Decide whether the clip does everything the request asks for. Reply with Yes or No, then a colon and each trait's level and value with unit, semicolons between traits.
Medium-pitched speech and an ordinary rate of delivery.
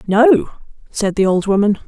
No: high, 210 Hz; average, 160 wpm